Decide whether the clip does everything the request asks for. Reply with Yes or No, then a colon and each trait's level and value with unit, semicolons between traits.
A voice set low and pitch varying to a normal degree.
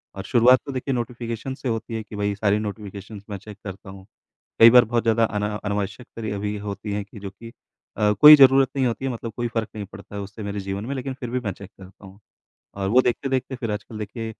Yes: low, 110 Hz; average, 3.0 semitones